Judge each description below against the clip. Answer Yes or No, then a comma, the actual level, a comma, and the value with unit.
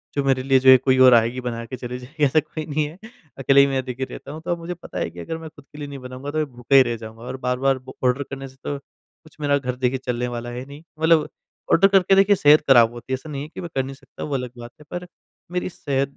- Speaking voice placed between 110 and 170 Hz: Yes, low, 135 Hz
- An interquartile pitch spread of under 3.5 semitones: Yes, average, 3.1 semitones